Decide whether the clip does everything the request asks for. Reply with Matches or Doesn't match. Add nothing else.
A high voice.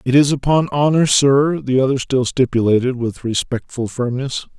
Doesn't match